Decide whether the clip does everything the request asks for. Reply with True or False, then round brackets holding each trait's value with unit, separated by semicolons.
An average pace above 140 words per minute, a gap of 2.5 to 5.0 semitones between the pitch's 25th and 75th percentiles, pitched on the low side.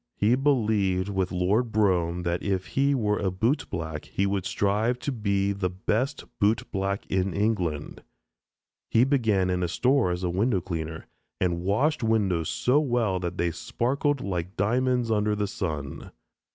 True (155 wpm; 4.1 semitones; 100 Hz)